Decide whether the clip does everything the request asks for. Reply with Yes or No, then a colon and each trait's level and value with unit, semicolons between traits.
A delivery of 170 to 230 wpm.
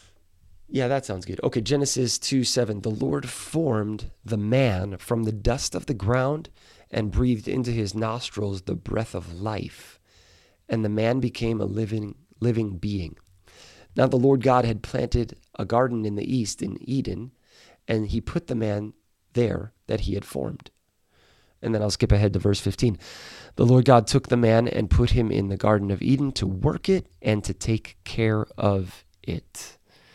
Yes: average, 180 wpm